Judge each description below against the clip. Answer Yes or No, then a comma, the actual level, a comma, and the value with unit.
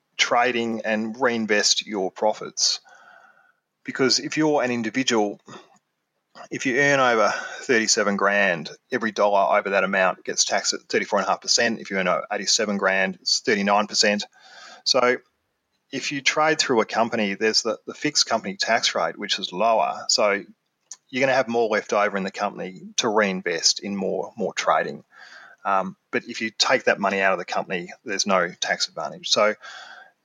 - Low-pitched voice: Yes, low, 110 Hz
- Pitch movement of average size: Yes, average, 3.2 semitones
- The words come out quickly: No, average, 165 wpm